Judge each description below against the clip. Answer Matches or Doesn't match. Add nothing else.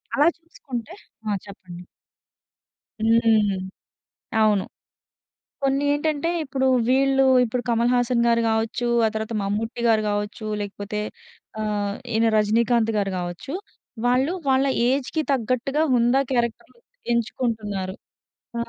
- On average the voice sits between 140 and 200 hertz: Doesn't match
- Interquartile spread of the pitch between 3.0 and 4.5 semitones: Matches